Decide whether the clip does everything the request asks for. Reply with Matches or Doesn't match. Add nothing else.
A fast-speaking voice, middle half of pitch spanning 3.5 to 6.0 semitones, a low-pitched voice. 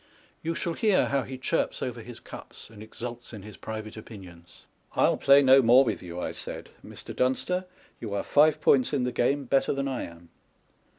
Matches